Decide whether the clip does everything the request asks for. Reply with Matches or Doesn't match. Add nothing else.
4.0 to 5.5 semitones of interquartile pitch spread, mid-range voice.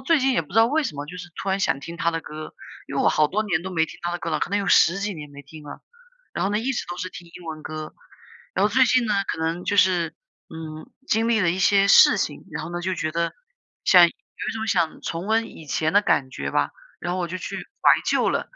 Matches